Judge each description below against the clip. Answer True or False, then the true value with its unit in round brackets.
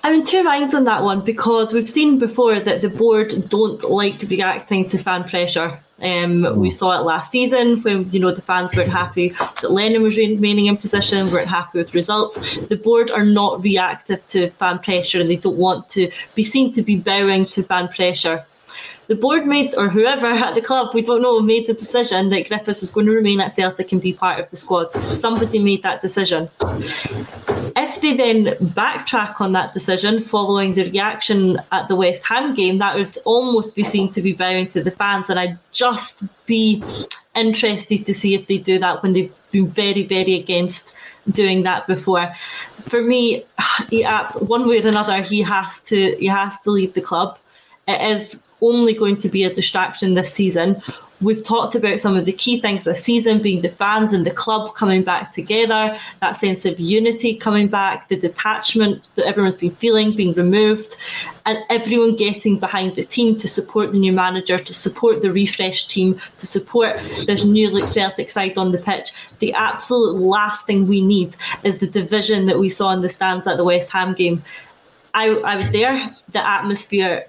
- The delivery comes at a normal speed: True (195 wpm)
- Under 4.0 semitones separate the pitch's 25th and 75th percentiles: True (2.8 semitones)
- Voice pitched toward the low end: False (200 Hz)